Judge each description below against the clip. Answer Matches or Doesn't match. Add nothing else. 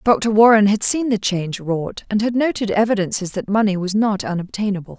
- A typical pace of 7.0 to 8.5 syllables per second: Doesn't match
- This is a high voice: Matches